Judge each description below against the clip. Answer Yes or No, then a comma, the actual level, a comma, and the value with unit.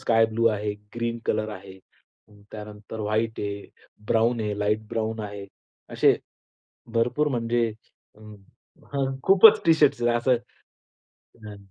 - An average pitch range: No, narrow, 2.1 semitones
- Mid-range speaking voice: No, low, 110 Hz